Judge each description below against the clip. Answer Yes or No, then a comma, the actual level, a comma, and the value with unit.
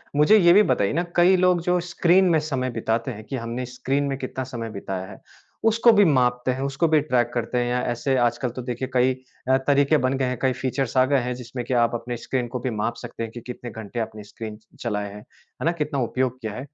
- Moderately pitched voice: No, low, 130 Hz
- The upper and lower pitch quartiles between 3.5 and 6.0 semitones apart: Yes, average, 3.9 semitones